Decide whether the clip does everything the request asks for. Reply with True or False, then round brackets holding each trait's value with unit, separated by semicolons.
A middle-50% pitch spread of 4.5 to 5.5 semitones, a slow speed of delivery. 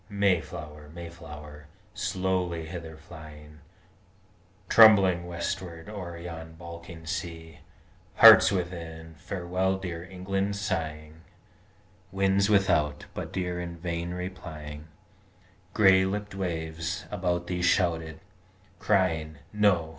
False (2.6 semitones; 95 wpm)